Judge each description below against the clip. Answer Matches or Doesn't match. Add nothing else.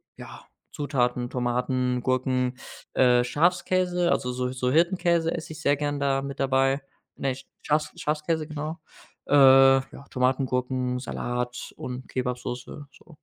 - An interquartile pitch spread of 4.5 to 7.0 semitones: Doesn't match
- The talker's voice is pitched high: Doesn't match